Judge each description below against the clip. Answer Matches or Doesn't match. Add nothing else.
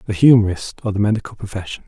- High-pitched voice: Doesn't match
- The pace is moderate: Matches